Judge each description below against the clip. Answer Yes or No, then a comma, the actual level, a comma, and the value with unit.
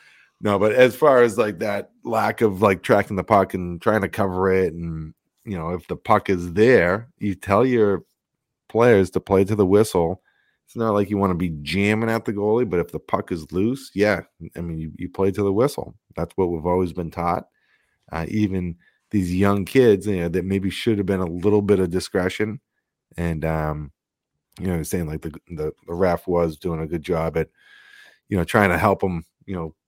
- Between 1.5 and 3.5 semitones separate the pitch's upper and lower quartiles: Yes, average, 3.2 semitones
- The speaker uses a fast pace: Yes, fast, 215 wpm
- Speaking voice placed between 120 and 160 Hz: No, very low, 95 Hz